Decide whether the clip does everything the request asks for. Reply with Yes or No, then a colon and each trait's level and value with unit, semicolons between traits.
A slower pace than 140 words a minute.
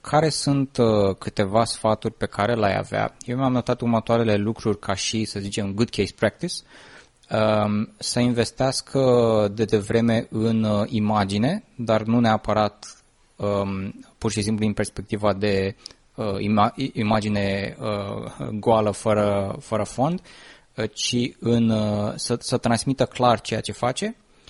Yes: average, 120 wpm